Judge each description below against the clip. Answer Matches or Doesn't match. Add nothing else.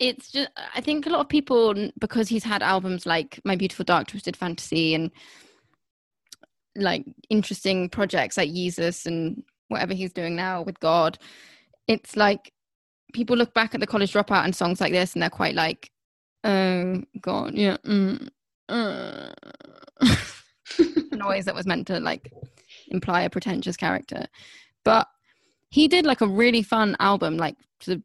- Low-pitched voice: Doesn't match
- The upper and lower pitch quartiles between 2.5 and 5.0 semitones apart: Doesn't match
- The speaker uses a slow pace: Doesn't match